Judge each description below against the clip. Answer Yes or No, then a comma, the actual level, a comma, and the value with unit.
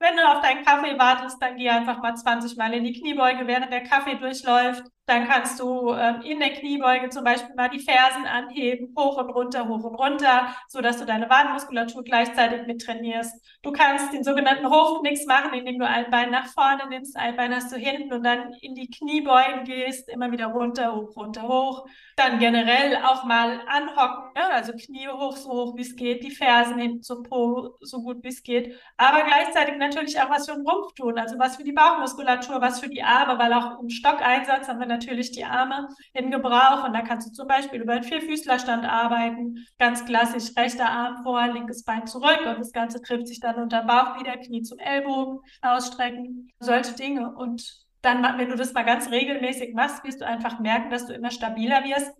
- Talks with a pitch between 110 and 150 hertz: No, very high, 250 Hz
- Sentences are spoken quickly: Yes, fast, 210 wpm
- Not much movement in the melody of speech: Yes, narrow, 2.1 semitones